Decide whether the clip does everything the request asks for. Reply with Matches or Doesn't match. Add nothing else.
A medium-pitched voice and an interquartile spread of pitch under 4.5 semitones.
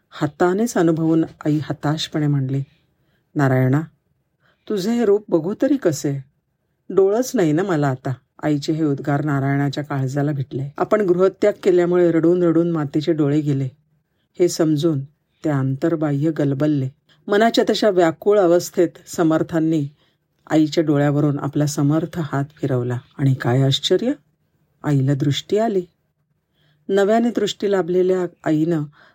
Matches